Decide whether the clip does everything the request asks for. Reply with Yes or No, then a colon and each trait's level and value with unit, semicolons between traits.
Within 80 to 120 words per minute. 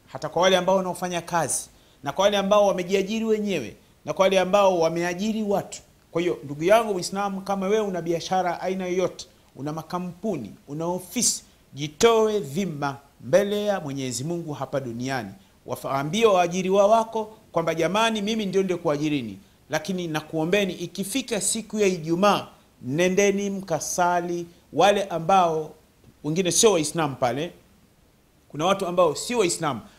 No: average, 135 wpm